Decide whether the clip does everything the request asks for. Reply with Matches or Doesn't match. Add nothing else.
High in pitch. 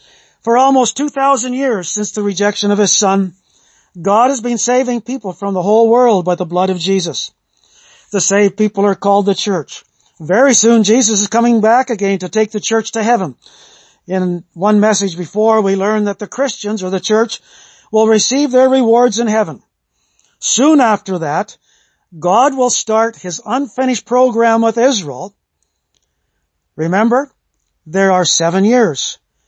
Matches